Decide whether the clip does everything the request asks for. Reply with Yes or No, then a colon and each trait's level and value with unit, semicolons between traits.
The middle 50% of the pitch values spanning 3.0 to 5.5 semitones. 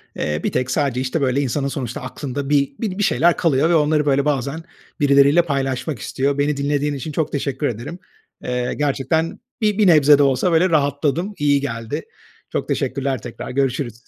No: narrow, 2.4 semitones